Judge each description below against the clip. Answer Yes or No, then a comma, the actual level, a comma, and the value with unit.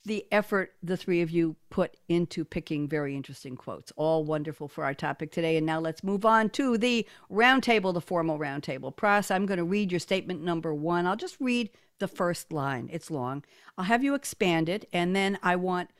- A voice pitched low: No, medium, 175 Hz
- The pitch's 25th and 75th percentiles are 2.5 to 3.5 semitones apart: No, average, 4.2 semitones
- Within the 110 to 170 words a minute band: No, fast, 205 wpm